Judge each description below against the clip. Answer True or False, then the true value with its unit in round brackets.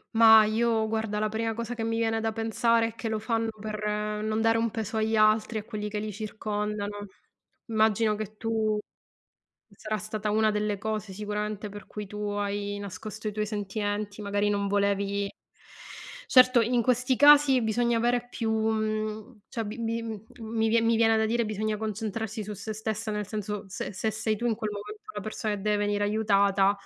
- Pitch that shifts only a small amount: True (1.4 semitones)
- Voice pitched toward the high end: True (215 Hz)